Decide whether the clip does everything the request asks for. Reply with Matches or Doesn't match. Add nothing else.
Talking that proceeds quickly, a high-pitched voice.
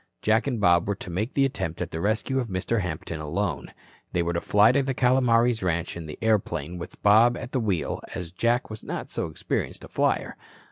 Doesn't match